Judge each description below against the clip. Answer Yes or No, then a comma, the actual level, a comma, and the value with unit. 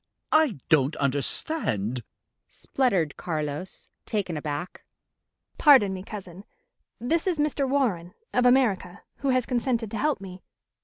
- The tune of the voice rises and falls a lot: Yes, wide, 8.0 semitones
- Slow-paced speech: Yes, slow, 120 wpm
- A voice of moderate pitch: No, high, 200 Hz